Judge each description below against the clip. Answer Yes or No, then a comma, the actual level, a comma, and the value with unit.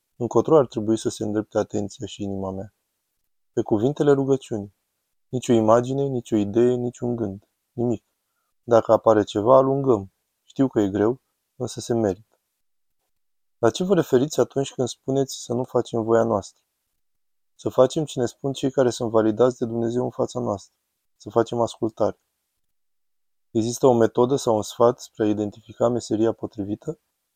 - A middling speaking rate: Yes, average, 160 wpm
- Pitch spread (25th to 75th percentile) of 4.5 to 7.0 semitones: No, average, 3.1 semitones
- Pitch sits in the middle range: No, low, 115 Hz